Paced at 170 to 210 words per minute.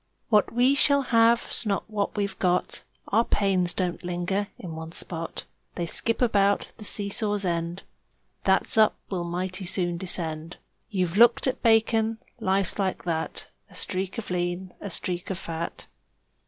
No: average, 155 wpm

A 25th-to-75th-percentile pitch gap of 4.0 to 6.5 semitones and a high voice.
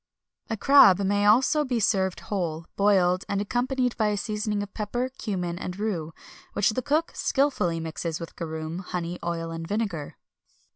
Yes: average, 4.6 semitones; high, 200 Hz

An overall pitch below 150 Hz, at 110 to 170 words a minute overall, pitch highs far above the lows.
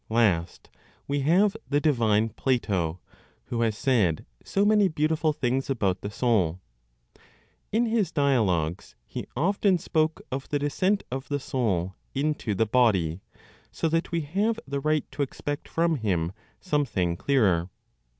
Yes: low, 135 Hz; average, 140 wpm; wide, 7.2 semitones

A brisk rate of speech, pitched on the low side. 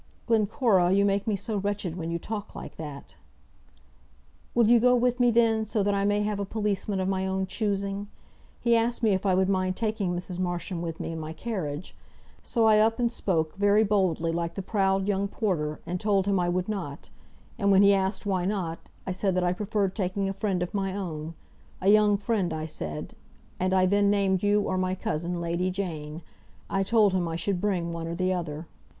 No: fast, 215 wpm; high, 195 Hz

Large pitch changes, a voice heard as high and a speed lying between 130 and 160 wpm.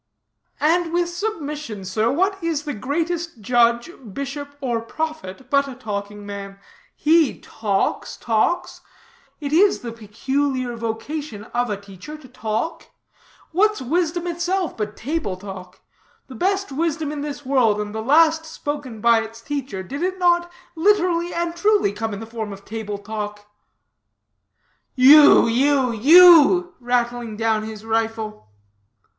Yes: wide, 6.7 semitones; very high, 265 Hz; average, 140 wpm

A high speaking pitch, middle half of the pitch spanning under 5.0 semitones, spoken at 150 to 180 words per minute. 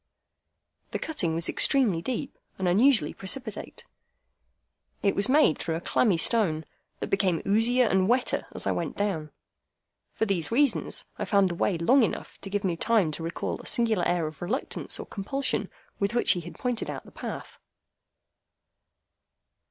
No: high, 200 Hz; wide, 5.6 semitones; average, 165 wpm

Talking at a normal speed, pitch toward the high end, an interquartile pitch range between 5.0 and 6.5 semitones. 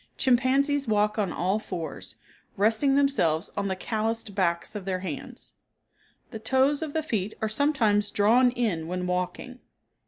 Yes: average, 150 wpm; high, 215 Hz; wide, 5.4 semitones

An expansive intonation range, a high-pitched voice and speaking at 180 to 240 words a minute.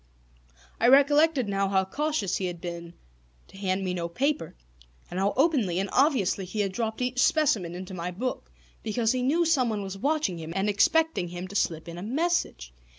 Yes: wide, 6.9 semitones; high, 200 Hz; average, 190 wpm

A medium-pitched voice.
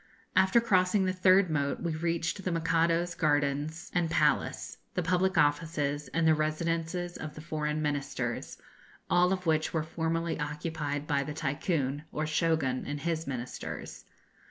Yes: medium, 160 Hz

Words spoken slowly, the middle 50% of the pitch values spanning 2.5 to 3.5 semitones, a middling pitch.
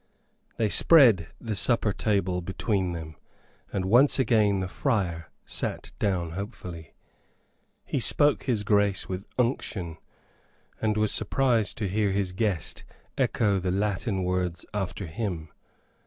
No: slow, 125 wpm; average, 3.2 semitones; low, 100 Hz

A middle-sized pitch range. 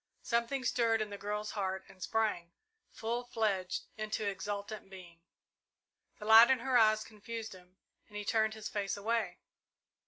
No: narrow, 2.2 semitones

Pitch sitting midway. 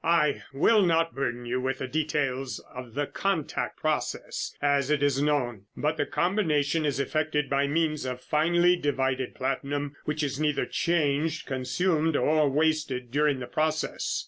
Yes: medium, 145 Hz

